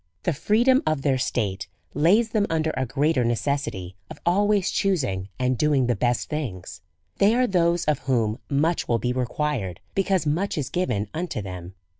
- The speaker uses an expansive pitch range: Yes, wide, 6.9 semitones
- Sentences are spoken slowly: No, average, 180 wpm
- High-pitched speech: No, medium, 145 Hz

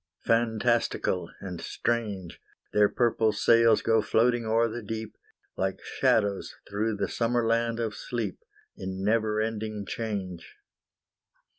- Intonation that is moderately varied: No, narrow, 2.2 semitones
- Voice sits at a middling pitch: No, low, 110 Hz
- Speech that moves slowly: Yes, slow, 120 wpm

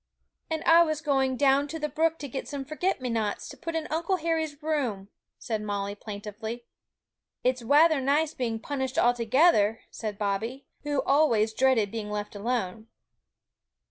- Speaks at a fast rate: No, average, 165 wpm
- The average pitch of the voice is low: No, very high, 260 Hz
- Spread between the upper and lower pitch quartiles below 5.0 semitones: No, wide, 5.6 semitones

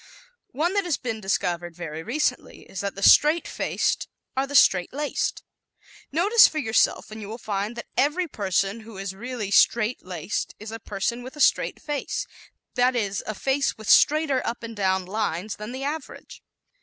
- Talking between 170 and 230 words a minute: Yes, average, 180 wpm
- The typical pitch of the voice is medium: No, high, 225 Hz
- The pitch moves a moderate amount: No, wide, 5.8 semitones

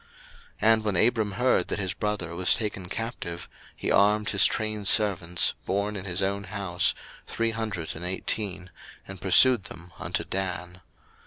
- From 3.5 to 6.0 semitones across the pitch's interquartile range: No, average, 2.9 semitones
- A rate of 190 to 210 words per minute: No, average, 160 wpm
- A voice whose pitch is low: Yes, low, 100 Hz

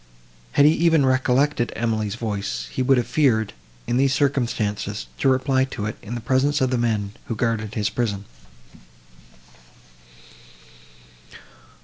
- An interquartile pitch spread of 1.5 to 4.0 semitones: Yes, average, 3.7 semitones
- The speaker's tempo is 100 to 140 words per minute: Yes, slow, 135 wpm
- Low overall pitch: Yes, low, 120 Hz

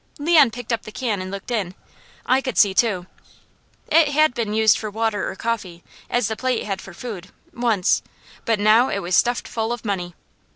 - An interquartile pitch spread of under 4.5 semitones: Yes, average, 3.6 semitones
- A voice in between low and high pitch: No, high, 220 Hz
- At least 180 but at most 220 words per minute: Yes, average, 200 wpm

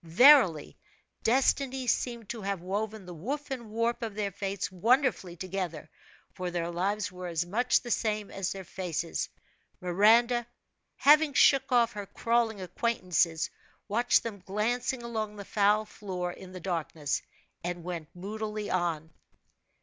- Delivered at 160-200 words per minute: No, average, 140 wpm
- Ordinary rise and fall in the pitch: Yes, average, 4.6 semitones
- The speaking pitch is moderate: No, high, 205 Hz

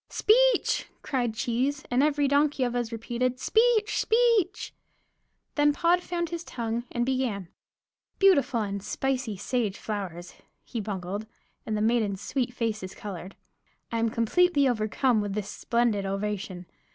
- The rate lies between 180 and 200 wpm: No, average, 140 wpm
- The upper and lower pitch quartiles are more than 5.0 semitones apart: Yes, wide, 5.4 semitones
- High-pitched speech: Yes, high, 240 Hz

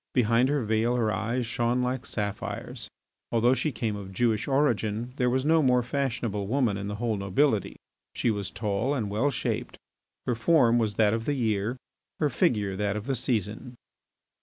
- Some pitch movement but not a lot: Yes, average, 3.3 semitones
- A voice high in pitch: No, low, 115 Hz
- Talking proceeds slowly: No, average, 180 wpm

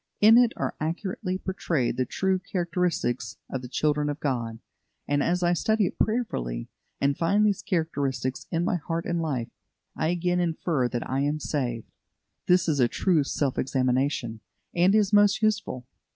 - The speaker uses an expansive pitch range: Yes, wide, 5.7 semitones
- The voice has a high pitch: No, medium, 160 Hz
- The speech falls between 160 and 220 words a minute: Yes, average, 165 wpm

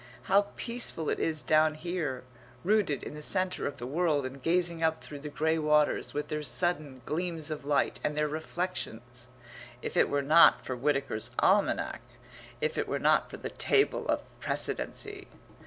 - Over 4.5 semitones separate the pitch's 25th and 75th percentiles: No, average, 3.6 semitones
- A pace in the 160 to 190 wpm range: Yes, average, 170 wpm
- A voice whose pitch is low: No, medium, 155 Hz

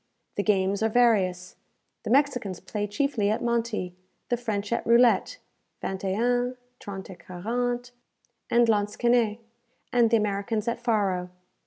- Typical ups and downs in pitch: Yes, average, 3.2 semitones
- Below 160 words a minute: Yes, average, 140 wpm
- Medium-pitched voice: No, high, 220 Hz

